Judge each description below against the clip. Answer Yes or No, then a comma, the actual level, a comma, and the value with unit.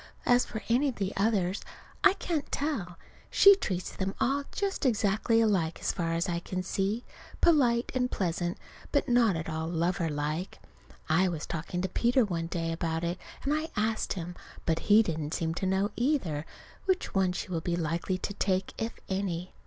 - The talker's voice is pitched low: No, high, 190 Hz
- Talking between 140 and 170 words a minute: No, average, 185 wpm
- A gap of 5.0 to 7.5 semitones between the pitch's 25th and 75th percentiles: Yes, wide, 5.6 semitones